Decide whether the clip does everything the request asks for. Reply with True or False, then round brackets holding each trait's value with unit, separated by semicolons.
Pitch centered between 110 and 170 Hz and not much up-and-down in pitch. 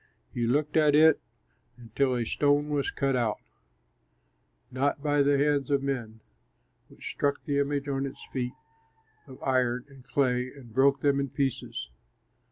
True (140 Hz; 2.2 semitones)